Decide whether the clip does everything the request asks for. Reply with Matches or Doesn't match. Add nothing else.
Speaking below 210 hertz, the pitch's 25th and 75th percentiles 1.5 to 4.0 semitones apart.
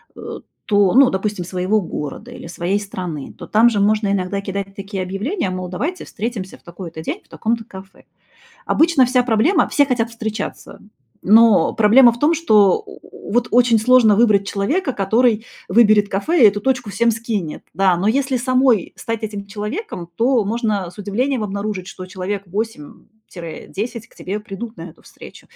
Doesn't match